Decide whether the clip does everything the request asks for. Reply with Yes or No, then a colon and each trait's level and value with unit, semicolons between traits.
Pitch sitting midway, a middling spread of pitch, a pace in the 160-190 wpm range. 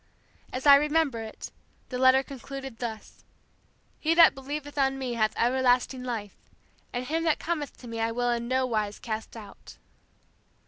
No: very high, 255 Hz; average, 3.3 semitones; average, 165 wpm